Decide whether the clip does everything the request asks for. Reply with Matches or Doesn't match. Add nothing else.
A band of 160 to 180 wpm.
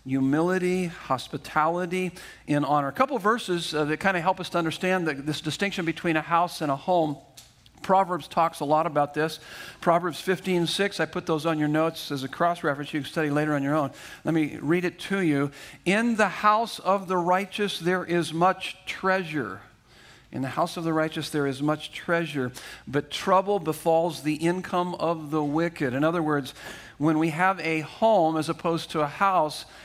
Doesn't match